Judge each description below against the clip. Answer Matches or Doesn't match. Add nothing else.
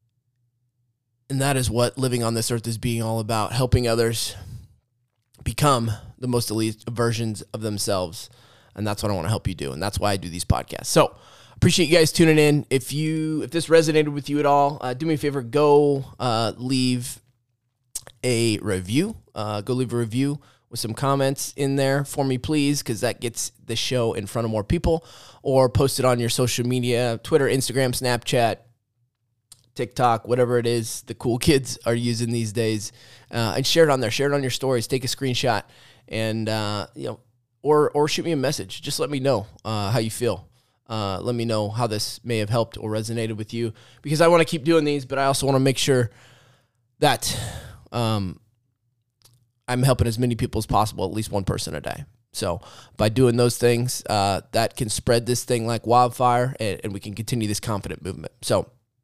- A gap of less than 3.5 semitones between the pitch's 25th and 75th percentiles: Matches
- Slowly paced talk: Doesn't match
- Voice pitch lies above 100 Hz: Matches